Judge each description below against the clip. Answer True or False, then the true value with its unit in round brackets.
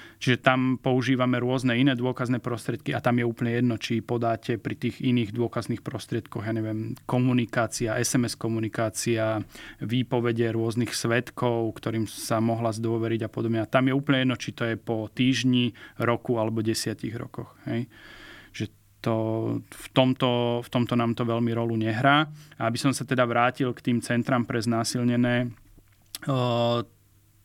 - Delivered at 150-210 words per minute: True (155 wpm)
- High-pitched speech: False (120 Hz)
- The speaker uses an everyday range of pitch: False (1.9 semitones)